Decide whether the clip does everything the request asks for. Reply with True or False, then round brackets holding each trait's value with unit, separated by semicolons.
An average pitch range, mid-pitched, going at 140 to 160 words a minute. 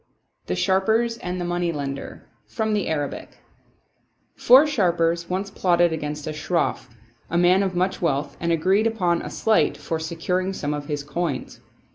True (3.3 semitones; 175 Hz; 155 wpm)